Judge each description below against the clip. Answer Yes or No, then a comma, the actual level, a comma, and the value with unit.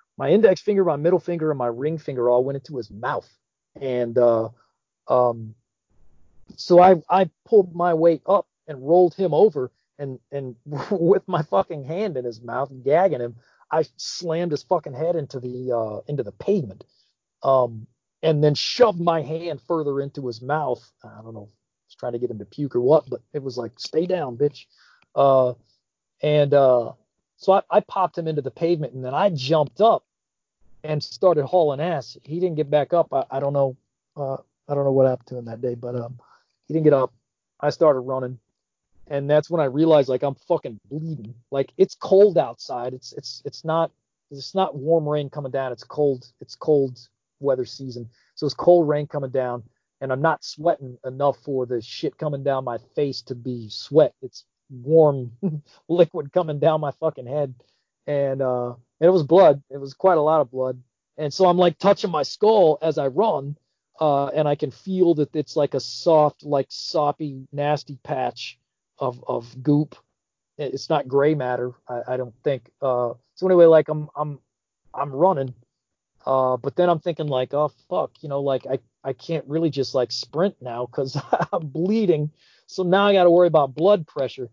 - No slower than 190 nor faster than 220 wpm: Yes, average, 195 wpm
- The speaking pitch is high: No, medium, 140 Hz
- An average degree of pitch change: Yes, average, 4.2 semitones